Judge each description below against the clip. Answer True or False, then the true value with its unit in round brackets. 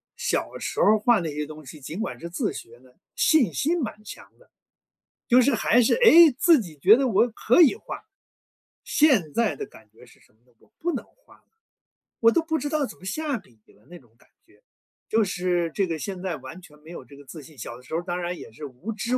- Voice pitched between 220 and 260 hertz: False (190 Hz)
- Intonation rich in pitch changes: True (8.8 semitones)